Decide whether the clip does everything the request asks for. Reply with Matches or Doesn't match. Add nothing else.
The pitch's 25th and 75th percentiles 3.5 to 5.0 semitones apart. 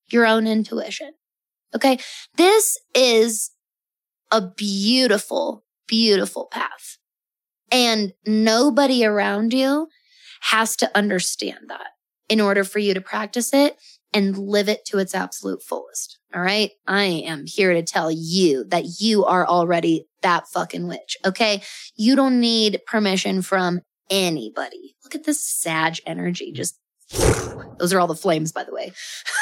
Matches